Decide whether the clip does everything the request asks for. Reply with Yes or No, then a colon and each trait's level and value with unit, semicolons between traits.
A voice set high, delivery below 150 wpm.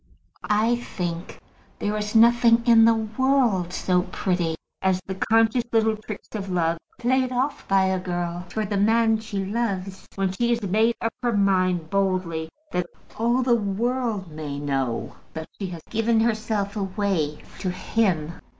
No: high, 200 Hz; average, 160 wpm